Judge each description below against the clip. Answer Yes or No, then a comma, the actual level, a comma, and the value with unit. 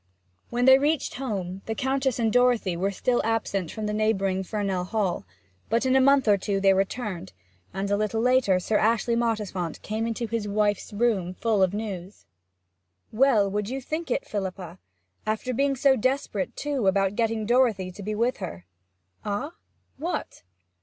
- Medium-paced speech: Yes, average, 170 wpm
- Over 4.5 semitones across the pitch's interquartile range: No, average, 4.1 semitones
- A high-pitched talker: Yes, high, 215 Hz